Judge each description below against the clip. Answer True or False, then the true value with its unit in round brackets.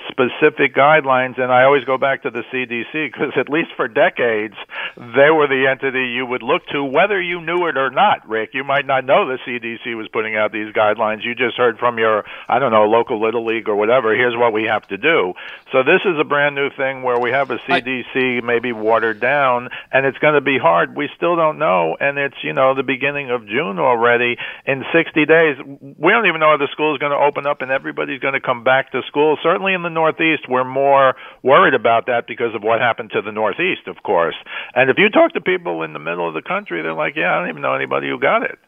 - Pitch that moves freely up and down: False (3.3 semitones)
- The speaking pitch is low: True (130 Hz)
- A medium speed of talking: False (245 wpm)